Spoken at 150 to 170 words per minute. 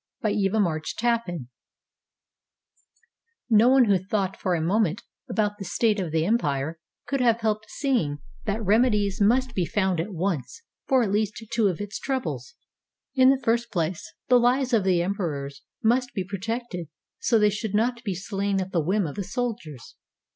No: average, 180 wpm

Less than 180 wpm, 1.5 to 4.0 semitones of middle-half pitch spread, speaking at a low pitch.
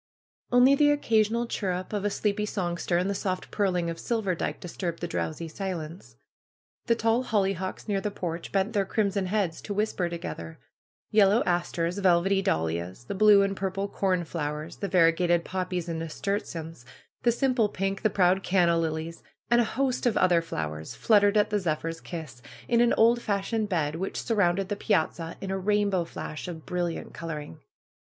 No: average, 170 wpm; average, 3.7 semitones; high, 190 Hz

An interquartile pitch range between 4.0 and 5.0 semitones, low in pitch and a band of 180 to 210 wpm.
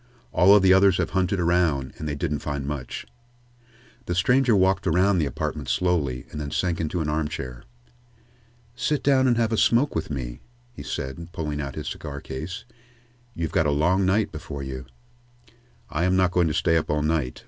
Yes: average, 4.3 semitones; very low, 80 Hz; average, 190 wpm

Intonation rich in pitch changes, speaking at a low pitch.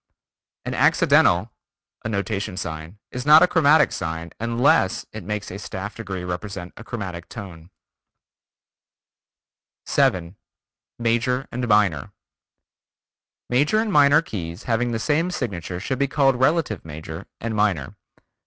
Yes: wide, 5.9 semitones; low, 105 Hz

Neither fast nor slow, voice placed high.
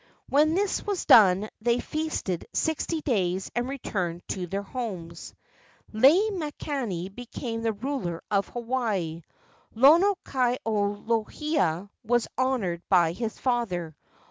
No: slow, 120 wpm; high, 230 Hz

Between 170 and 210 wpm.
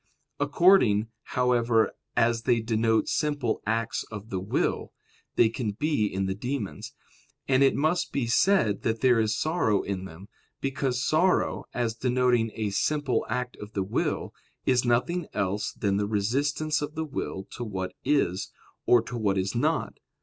No: average, 160 wpm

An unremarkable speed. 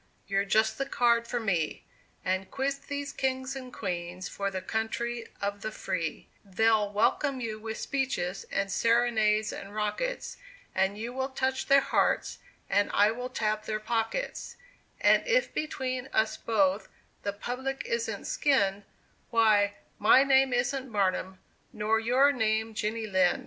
Yes: average, 150 wpm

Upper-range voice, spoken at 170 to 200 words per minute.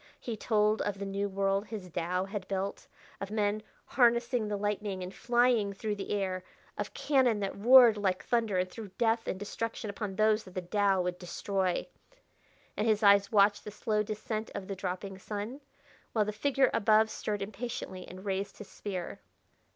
Yes: high, 205 Hz; average, 180 wpm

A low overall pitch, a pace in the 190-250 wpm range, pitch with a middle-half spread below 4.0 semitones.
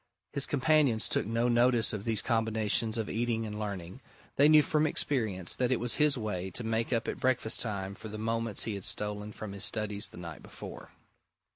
Yes: low, 110 Hz; fast, 205 wpm; average, 2.7 semitones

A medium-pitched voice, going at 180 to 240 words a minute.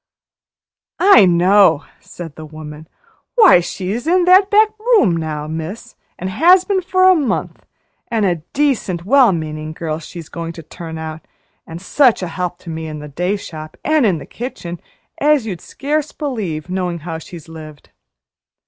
No: medium, 180 Hz; average, 170 wpm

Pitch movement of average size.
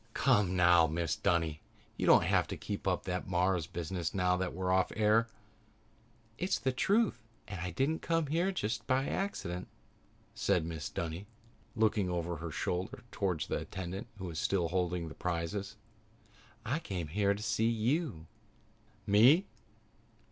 Yes: average, 4.4 semitones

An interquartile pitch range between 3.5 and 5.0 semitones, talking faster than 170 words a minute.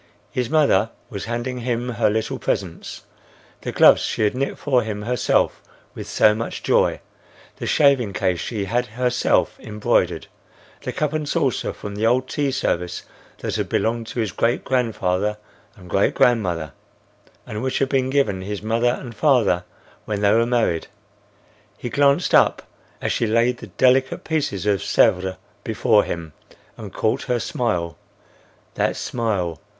No: average, 3.9 semitones; average, 155 wpm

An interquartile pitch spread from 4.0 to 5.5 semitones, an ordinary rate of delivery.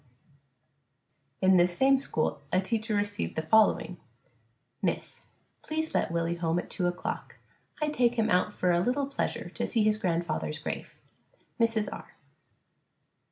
Yes: average, 5.0 semitones; average, 155 wpm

